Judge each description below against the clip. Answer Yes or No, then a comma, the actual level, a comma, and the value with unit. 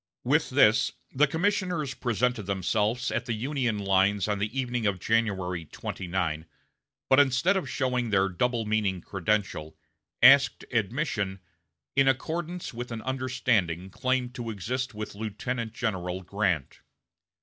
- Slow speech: Yes, slow, 130 wpm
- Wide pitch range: No, average, 4.9 semitones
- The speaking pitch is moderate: No, low, 110 Hz